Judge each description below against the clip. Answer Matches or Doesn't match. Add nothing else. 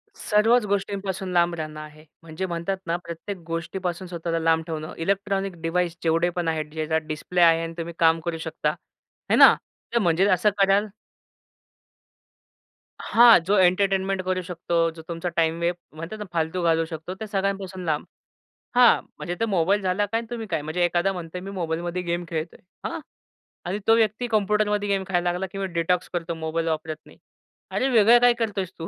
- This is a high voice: Doesn't match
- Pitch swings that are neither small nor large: Matches